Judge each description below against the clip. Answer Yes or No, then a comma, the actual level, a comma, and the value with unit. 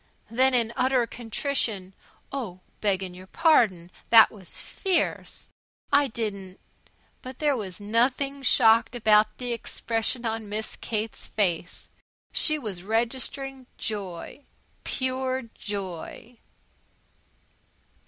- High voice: Yes, high, 225 Hz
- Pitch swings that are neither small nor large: Yes, average, 4.2 semitones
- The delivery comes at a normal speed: No, slow, 105 wpm